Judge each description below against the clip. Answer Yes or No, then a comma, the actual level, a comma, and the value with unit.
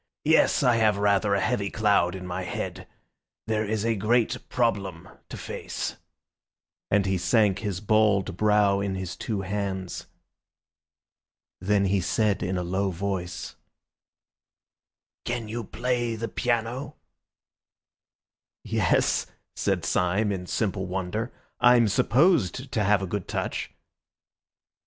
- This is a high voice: No, low, 105 Hz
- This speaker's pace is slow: Yes, slow, 125 wpm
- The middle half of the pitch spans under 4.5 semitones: Yes, average, 3.0 semitones